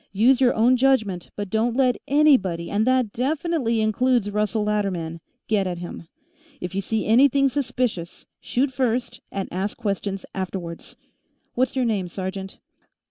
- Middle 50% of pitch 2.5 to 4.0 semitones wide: No, average, 4.8 semitones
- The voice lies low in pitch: No, high, 220 Hz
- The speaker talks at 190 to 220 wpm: No, average, 145 wpm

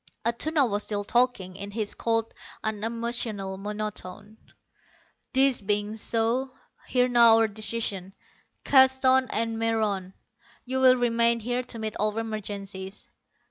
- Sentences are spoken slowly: Yes, slow, 120 wpm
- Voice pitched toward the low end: No, high, 225 Hz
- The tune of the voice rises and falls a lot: No, average, 2.9 semitones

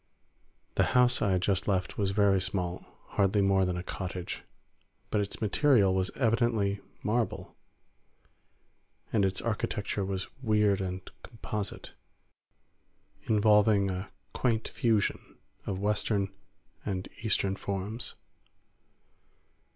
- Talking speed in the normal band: No, slow, 105 wpm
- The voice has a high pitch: No, low, 100 Hz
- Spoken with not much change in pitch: Yes, narrow, 2.2 semitones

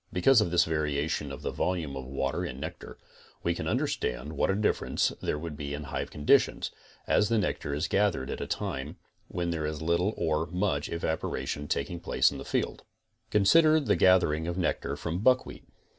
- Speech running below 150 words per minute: No, average, 195 wpm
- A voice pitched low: Yes, very low, 80 Hz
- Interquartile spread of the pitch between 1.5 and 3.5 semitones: No, average, 4.1 semitones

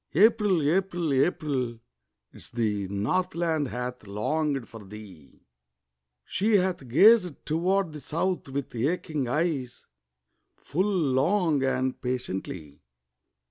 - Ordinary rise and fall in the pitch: No, wide, 6.3 semitones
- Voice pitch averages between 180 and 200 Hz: No, medium, 145 Hz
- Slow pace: Yes, slow, 100 wpm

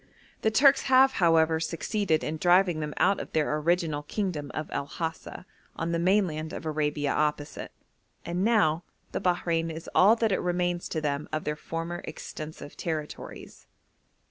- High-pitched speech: No, medium, 165 Hz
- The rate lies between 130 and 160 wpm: Yes, average, 155 wpm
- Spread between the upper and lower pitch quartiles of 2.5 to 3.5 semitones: Yes, average, 2.8 semitones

